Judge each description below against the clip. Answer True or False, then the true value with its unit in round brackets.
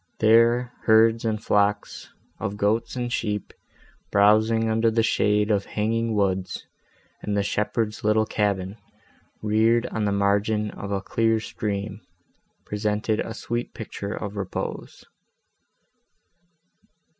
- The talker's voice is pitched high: False (105 Hz)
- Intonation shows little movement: True (1.7 semitones)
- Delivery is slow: True (120 wpm)